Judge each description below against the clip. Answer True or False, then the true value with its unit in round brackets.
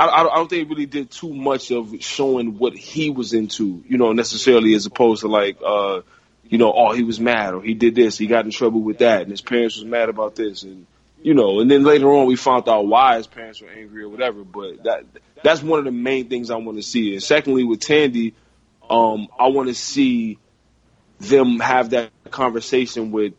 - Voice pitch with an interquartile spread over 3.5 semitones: False (3.2 semitones)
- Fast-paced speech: True (230 wpm)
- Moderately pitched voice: False (120 Hz)